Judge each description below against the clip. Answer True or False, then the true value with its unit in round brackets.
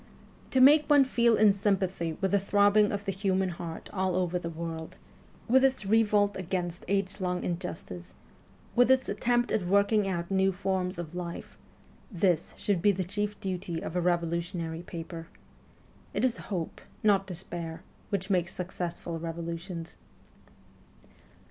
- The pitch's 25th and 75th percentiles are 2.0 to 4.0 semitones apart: True (3.0 semitones)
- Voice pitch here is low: False (185 Hz)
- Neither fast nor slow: True (150 wpm)